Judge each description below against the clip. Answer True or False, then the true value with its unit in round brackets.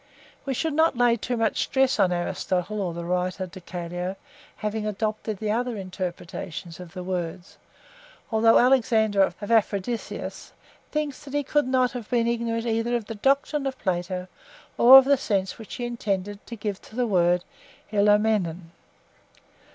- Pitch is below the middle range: False (215 Hz)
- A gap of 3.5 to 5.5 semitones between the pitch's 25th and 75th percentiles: True (4.5 semitones)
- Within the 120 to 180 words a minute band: True (165 wpm)